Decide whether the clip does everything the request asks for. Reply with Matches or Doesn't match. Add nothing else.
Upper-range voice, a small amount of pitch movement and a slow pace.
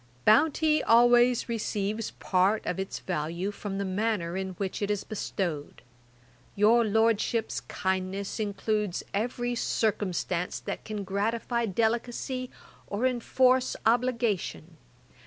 Doesn't match